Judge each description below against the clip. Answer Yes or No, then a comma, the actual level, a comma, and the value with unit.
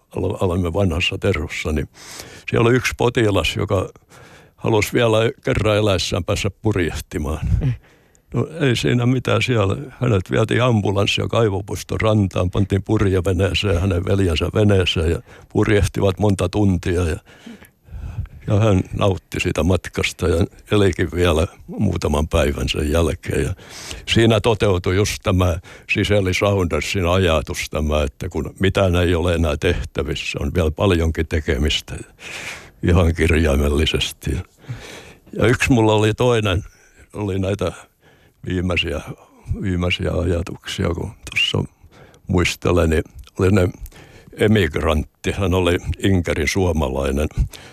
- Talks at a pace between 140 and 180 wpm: No, average, 115 wpm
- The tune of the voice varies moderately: Yes, average, 3.4 semitones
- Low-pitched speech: Yes, very low, 95 Hz